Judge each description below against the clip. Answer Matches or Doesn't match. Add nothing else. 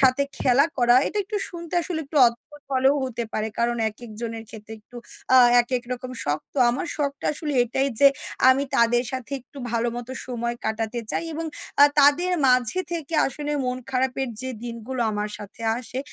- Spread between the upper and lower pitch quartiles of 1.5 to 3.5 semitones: Matches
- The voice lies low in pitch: Doesn't match